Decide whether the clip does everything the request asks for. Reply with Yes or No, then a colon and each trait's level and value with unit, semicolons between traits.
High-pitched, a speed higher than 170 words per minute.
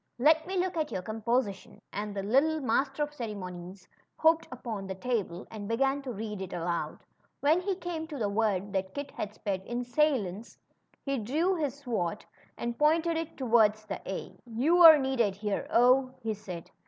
Yes: high, 235 Hz; average, 180 wpm